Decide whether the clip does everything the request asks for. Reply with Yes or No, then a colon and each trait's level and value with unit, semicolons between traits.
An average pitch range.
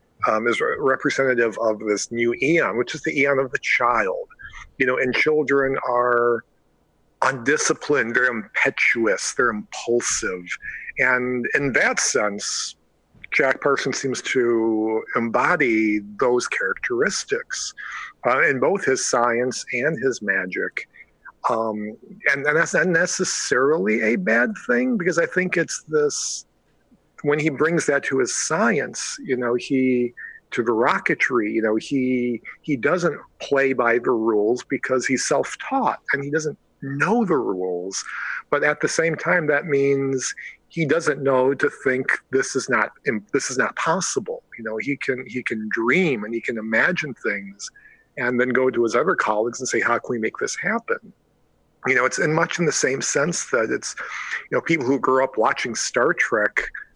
Yes: average, 4.0 semitones